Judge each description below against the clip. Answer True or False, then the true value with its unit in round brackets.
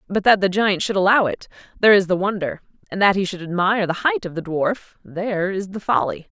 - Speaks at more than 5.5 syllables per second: True (6.0 syllables/s)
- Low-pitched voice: False (195 Hz)